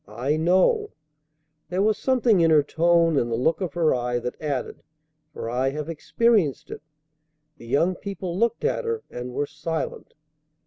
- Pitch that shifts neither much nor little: No, wide, 6.1 semitones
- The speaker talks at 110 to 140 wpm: No, average, 170 wpm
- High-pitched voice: No, medium, 165 Hz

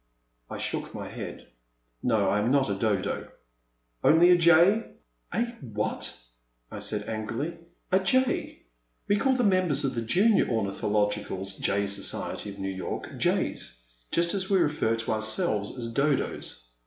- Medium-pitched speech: No, low, 115 Hz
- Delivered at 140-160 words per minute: Yes, average, 155 wpm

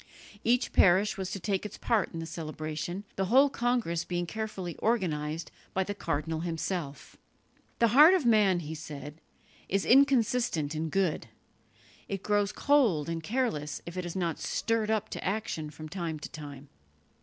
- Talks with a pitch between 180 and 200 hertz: Yes, medium, 185 Hz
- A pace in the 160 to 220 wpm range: Yes, average, 165 wpm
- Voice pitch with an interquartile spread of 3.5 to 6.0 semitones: Yes, wide, 5.4 semitones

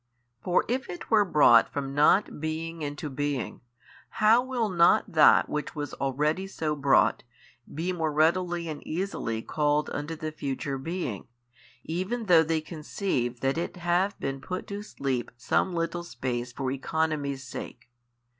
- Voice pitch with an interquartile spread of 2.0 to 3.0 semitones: No, average, 4.2 semitones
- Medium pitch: Yes, medium, 155 Hz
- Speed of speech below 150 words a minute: No, average, 155 wpm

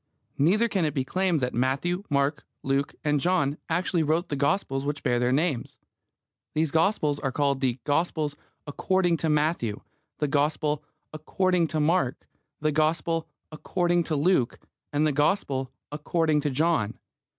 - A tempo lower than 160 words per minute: Yes, average, 150 wpm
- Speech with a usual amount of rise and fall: Yes, average, 3.3 semitones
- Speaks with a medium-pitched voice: Yes, medium, 150 Hz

